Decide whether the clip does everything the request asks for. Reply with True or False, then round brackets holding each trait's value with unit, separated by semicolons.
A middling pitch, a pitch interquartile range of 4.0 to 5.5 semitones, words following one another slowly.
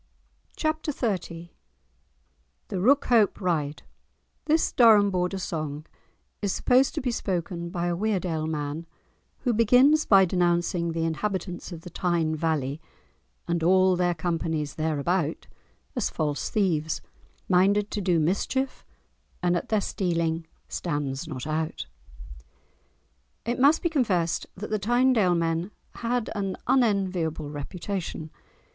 True (180 Hz; 4.5 semitones; 125 wpm)